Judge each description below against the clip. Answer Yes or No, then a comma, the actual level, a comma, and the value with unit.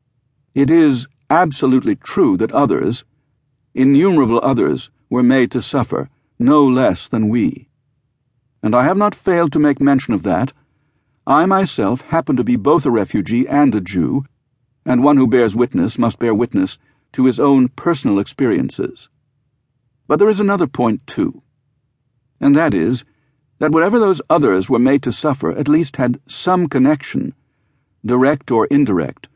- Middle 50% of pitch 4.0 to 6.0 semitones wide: No, narrow, 2.6 semitones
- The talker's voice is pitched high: No, low, 135 Hz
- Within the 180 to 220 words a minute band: No, average, 155 wpm